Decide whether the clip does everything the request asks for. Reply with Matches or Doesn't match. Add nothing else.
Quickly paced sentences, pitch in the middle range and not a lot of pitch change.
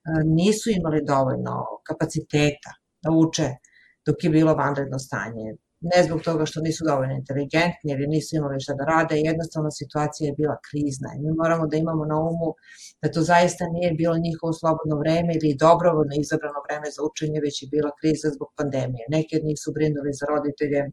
Matches